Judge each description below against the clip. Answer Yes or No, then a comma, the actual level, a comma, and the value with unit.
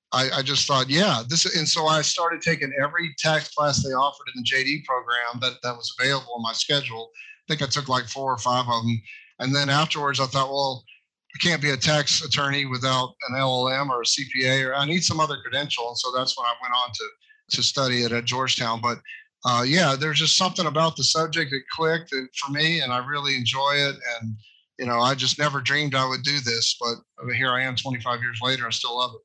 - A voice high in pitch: No, low, 135 Hz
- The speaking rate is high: Yes, fast, 230 wpm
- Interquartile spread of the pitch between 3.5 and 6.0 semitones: No, average, 3.0 semitones